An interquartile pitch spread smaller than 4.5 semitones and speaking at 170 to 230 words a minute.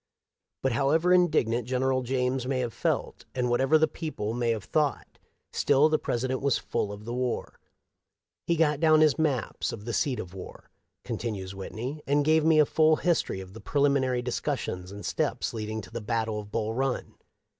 No: average, 4.8 semitones; average, 190 wpm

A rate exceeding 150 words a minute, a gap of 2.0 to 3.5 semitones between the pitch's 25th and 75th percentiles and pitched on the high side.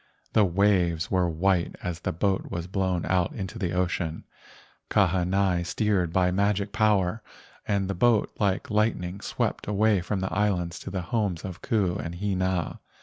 No: average, 165 wpm; narrow, 2.5 semitones; very low, 95 Hz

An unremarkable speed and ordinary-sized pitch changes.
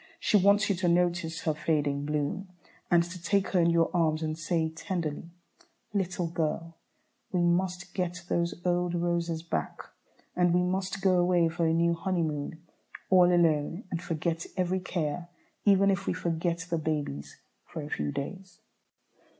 No: average, 160 wpm; narrow, 2.0 semitones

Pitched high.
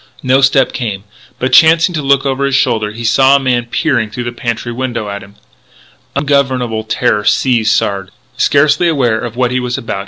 No: low, 125 Hz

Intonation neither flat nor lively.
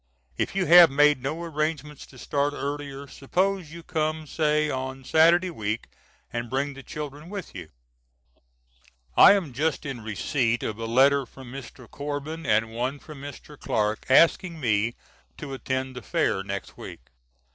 Yes: average, 3.7 semitones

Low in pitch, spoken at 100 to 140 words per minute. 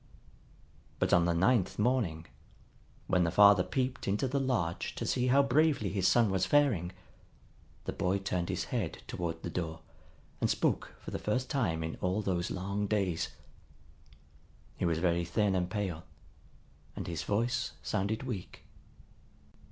No: very low, 95 Hz; average, 150 wpm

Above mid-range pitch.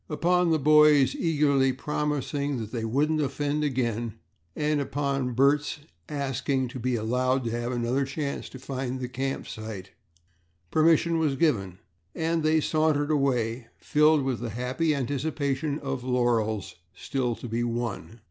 No: low, 135 Hz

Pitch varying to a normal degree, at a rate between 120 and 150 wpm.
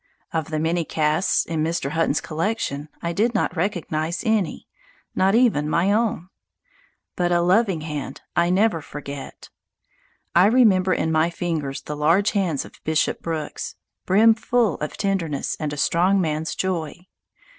Yes: average, 3.9 semitones; average, 145 wpm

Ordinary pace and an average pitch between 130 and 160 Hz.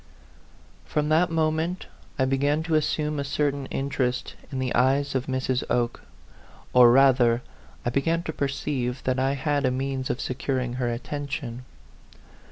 Yes: average, 150 wpm; low, 135 Hz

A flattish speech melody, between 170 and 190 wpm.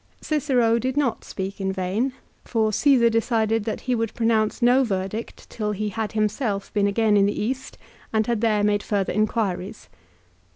Yes: narrow, 2.3 semitones; average, 175 wpm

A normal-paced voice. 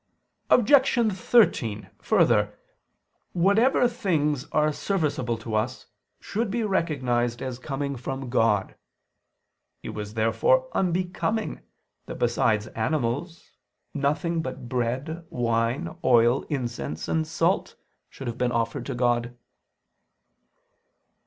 No: slow, 100 wpm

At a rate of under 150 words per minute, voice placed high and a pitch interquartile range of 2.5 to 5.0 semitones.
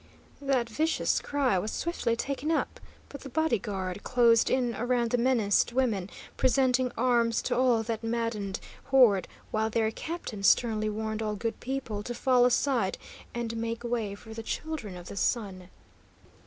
No: average, 160 wpm; high, 235 Hz; average, 2.9 semitones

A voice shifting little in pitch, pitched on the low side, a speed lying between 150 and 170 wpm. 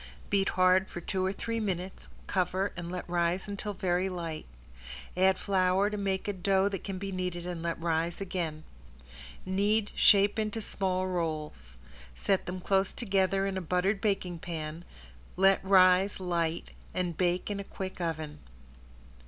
No: narrow, 2.0 semitones; medium, 185 Hz; average, 160 wpm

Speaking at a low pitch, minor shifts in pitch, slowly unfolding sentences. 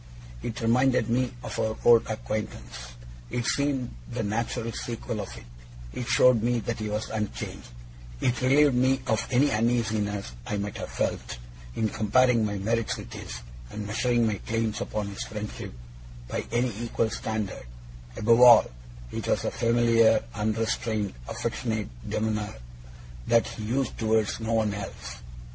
No: low, 115 Hz; narrow, 2.0 semitones; average, 150 wpm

